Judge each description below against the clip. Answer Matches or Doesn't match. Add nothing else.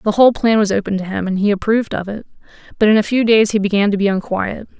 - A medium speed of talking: Doesn't match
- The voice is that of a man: Doesn't match